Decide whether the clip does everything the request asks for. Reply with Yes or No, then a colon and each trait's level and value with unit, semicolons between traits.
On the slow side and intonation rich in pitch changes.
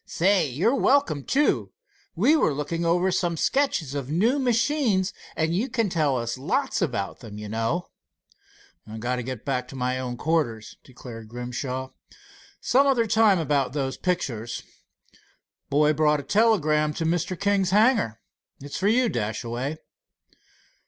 No: average, 145 wpm; wide, 8.0 semitones